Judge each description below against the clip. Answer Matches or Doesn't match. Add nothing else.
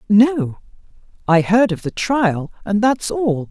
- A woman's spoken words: Matches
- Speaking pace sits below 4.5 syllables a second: Matches